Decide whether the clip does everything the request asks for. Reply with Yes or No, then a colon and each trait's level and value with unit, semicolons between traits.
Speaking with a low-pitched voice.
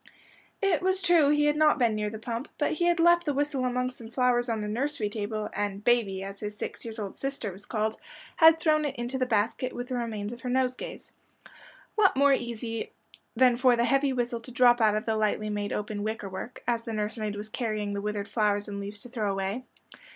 No: high, 235 Hz